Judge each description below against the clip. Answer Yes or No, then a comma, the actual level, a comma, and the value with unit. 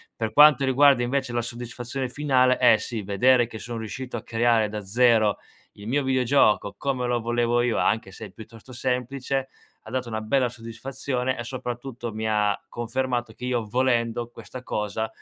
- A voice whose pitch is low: Yes, low, 120 Hz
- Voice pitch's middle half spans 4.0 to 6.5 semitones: No, narrow, 2.5 semitones